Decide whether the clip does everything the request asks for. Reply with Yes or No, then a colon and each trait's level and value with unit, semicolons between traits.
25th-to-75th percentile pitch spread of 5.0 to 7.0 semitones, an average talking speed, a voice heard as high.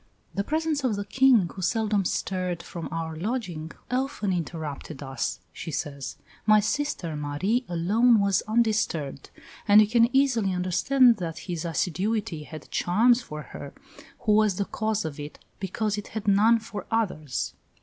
Yes: average, 5.3 semitones; average, 155 wpm; high, 200 Hz